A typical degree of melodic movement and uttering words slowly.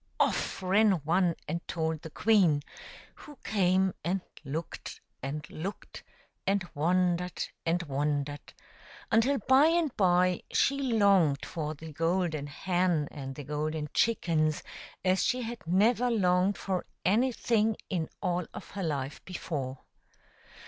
Yes: average, 4.6 semitones; slow, 130 wpm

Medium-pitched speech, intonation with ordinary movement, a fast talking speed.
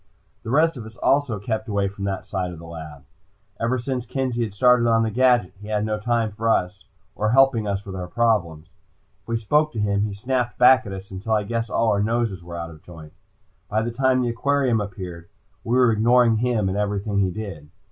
No: low, 110 Hz; average, 3.6 semitones; fast, 225 wpm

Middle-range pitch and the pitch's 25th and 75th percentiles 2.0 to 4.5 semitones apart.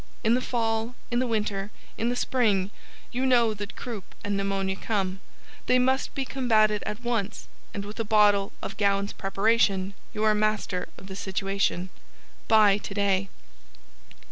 No: high, 210 Hz; narrow, 2.6 semitones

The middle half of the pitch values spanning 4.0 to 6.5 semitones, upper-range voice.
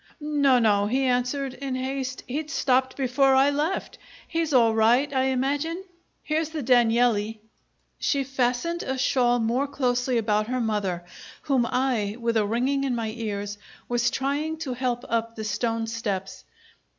No: average, 3.2 semitones; very high, 250 Hz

